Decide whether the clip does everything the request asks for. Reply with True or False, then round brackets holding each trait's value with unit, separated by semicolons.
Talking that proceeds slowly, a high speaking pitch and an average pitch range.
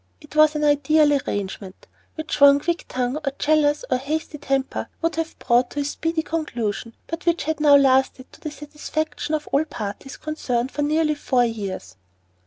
False (175 wpm; 290 Hz; 3.3 semitones)